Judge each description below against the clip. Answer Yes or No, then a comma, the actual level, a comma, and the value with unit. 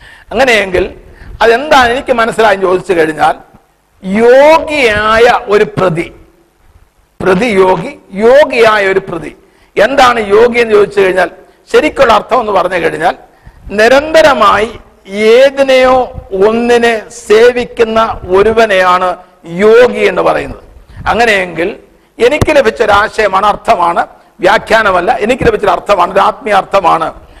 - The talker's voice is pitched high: Yes, high, 215 Hz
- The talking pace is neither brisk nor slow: No, slow, 90 wpm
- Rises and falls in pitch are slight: No, average, 4.2 semitones